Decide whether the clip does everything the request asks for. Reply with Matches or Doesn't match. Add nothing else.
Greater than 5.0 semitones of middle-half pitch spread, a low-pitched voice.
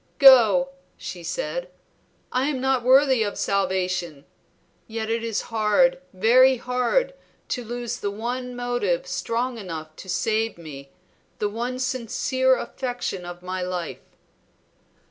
Doesn't match